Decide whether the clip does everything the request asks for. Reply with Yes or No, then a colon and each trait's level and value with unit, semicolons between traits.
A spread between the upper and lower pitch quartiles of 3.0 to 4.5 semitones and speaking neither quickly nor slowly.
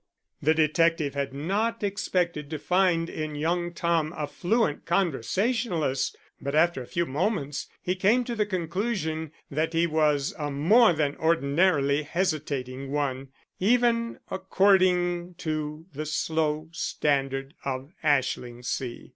No: average, 4.2 semitones; slow, 125 wpm